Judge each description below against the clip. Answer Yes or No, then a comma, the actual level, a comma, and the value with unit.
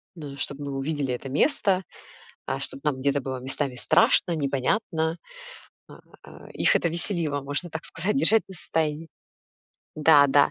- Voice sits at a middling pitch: Yes, medium, 150 Hz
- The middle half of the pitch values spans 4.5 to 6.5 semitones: No, average, 3.3 semitones